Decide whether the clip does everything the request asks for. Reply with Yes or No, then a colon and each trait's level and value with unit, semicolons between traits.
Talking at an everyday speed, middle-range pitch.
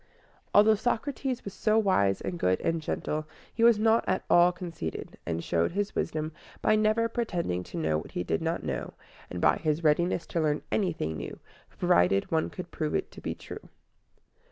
Yes: average, 185 wpm; medium, 170 Hz